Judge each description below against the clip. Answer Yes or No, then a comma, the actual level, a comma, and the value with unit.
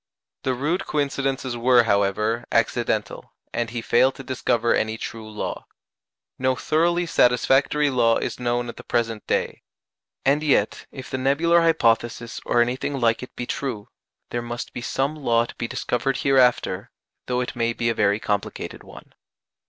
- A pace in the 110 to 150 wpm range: No, average, 160 wpm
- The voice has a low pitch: Yes, low, 120 Hz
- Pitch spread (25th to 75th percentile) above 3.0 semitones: No, average, 2.7 semitones